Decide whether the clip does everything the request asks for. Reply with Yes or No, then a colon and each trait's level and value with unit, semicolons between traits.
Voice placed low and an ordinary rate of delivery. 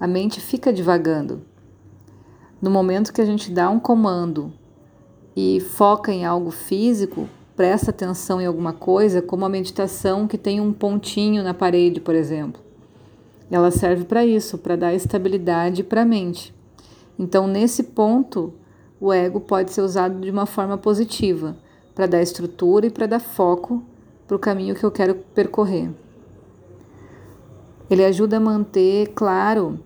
No: high, 190 Hz; average, 150 wpm